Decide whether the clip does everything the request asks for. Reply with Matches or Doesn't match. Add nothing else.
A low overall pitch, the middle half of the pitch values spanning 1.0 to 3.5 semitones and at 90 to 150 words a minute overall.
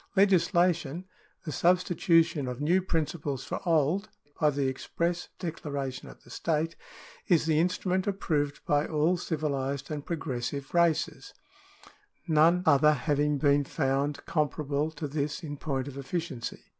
Doesn't match